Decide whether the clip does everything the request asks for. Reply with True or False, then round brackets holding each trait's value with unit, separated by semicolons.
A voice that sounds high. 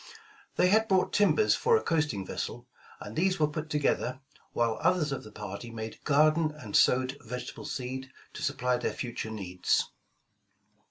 False (130 Hz)